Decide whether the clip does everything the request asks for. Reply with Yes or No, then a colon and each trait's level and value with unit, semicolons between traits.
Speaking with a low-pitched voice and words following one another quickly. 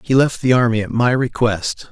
Yes: low, 120 Hz; fast, 220 wpm